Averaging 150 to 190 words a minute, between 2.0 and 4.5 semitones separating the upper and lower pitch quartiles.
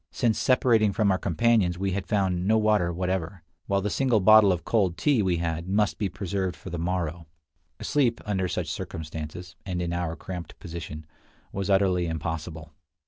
Yes: average, 175 wpm; average, 3.3 semitones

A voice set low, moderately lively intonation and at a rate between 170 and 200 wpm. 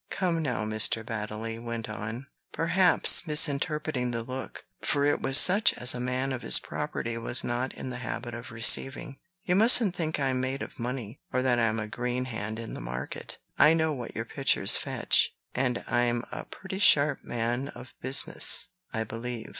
Yes: low, 125 Hz; average, 3.7 semitones; average, 180 wpm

